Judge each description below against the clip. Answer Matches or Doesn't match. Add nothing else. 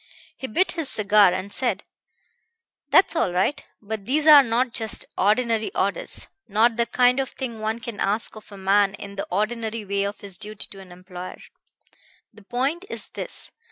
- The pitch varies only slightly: Doesn't match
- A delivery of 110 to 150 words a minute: Doesn't match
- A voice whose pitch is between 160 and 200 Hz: Doesn't match